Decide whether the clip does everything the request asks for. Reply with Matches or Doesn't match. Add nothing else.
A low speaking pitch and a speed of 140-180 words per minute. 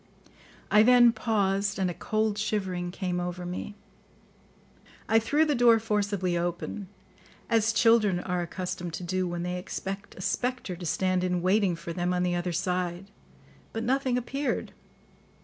Doesn't match